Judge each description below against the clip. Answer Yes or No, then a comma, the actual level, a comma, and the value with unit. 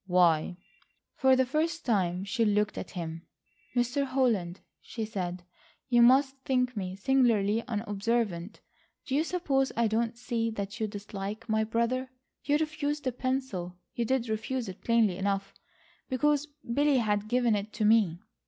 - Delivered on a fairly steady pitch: No, average, 4.5 semitones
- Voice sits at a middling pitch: No, high, 230 Hz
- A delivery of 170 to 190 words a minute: No, average, 145 wpm